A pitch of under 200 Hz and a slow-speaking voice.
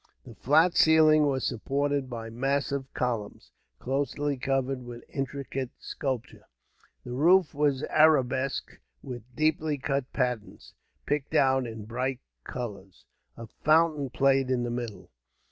Yes: low, 135 Hz; slow, 125 wpm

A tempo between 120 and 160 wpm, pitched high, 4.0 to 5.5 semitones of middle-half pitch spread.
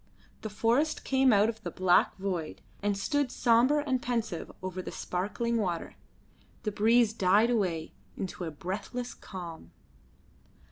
Yes: average, 140 wpm; high, 210 Hz; average, 4.5 semitones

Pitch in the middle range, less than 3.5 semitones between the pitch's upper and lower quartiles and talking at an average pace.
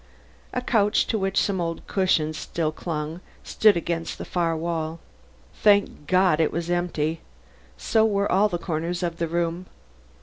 Yes: medium, 170 Hz; average, 2.8 semitones; average, 160 wpm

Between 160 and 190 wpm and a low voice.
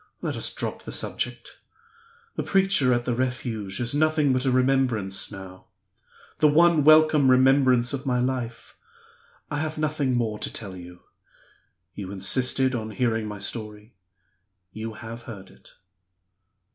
No: average, 145 wpm; low, 125 Hz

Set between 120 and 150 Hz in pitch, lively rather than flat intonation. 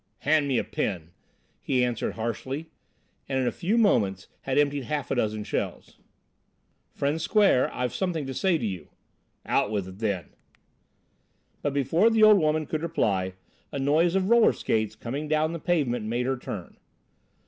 Yes: low, 135 Hz; wide, 6.3 semitones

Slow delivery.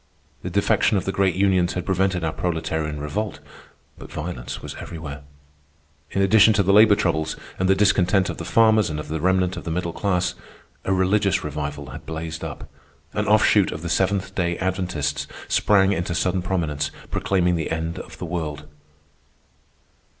No: average, 170 wpm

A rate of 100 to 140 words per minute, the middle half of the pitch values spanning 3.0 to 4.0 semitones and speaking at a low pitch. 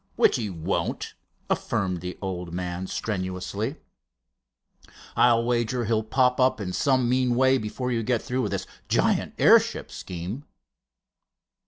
No: slow, 135 wpm; wide, 5.4 semitones; low, 115 Hz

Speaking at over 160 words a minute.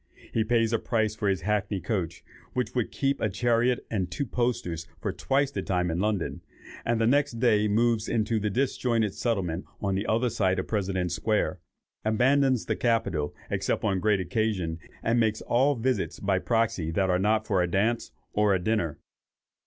Yes: average, 185 wpm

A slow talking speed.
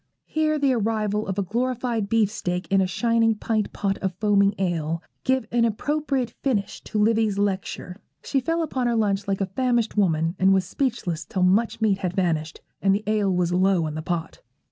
No: average, 190 wpm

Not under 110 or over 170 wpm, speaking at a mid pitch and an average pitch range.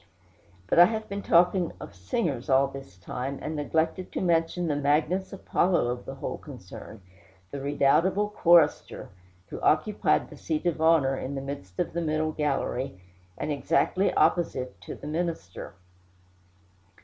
Yes: average, 150 wpm; medium, 150 Hz; average, 4.2 semitones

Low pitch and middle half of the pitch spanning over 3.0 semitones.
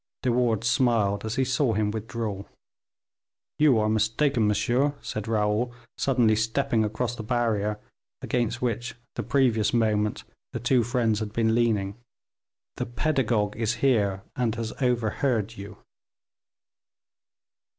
No: low, 115 Hz; narrow, 2.5 semitones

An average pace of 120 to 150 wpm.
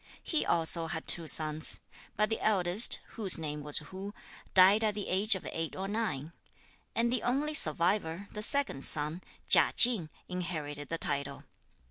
No: average, 160 wpm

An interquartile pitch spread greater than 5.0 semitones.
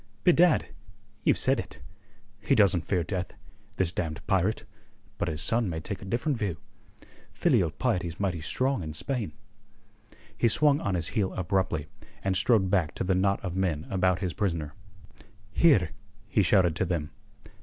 No: average, 3.8 semitones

